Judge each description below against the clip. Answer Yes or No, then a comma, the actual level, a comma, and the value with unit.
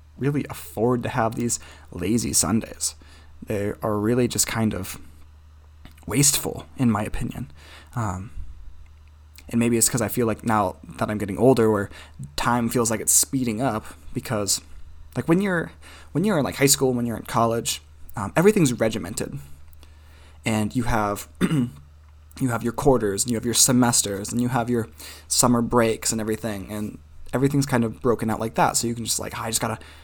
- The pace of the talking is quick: No, average, 180 wpm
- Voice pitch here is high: No, low, 110 Hz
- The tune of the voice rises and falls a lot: Yes, wide, 7.5 semitones